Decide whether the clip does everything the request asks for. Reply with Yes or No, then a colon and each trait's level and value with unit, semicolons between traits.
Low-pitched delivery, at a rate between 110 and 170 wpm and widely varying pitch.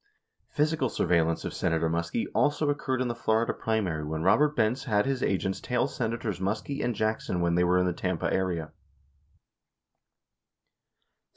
Yes: low, 105 Hz; average, 160 wpm; wide, 6.2 semitones